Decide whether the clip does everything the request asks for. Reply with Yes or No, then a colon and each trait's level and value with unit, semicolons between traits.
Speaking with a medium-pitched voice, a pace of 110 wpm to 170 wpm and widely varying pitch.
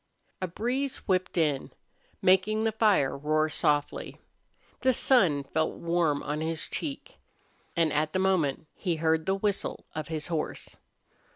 No: medium, 165 Hz; average, 145 wpm; average, 4.2 semitones